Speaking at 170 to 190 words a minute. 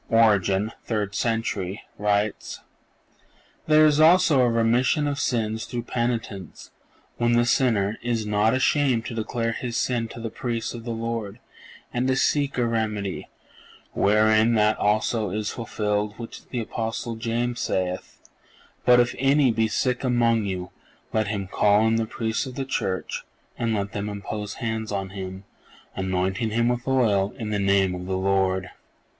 No: average, 160 wpm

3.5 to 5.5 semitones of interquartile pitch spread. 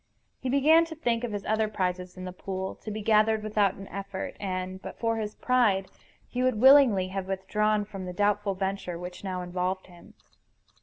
No: average, 2.7 semitones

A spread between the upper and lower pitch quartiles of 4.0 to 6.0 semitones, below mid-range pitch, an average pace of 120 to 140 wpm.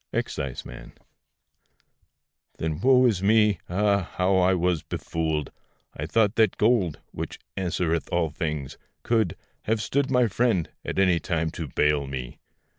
Yes: average, 5.2 semitones; very low, 90 Hz; slow, 135 wpm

